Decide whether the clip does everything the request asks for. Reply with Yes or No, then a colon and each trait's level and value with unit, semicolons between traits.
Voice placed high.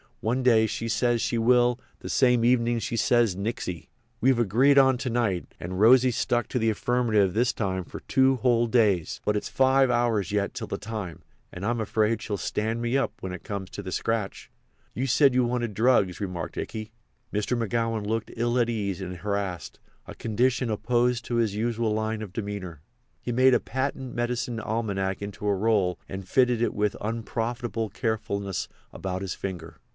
No: low, 115 Hz